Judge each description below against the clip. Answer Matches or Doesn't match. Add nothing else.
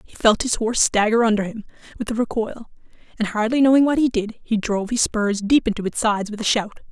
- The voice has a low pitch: Doesn't match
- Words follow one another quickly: Matches